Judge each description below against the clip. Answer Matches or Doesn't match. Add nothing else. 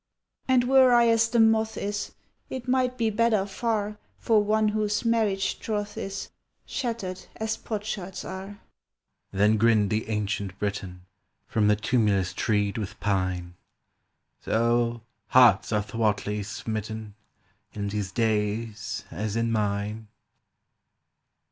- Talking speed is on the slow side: Matches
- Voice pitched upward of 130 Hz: Doesn't match